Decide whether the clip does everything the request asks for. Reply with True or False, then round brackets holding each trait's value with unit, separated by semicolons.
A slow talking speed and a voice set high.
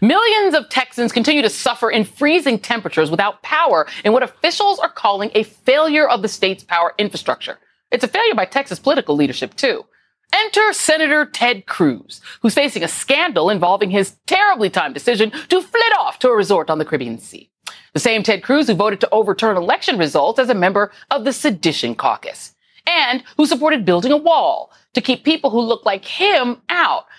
False (190 wpm; 245 Hz)